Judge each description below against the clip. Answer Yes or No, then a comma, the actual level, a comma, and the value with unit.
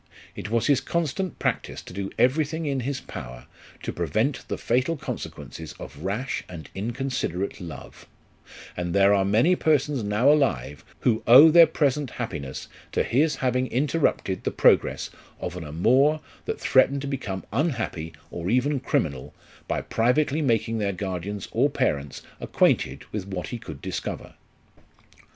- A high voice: No, low, 115 Hz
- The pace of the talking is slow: No, average, 150 wpm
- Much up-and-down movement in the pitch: Yes, wide, 7.1 semitones